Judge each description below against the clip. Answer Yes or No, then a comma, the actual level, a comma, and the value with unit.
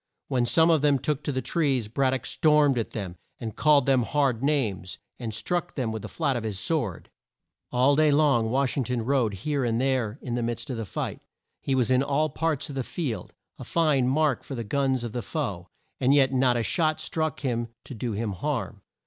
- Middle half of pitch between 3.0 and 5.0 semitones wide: Yes, average, 3.9 semitones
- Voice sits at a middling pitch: No, low, 130 Hz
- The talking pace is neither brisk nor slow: No, fast, 225 wpm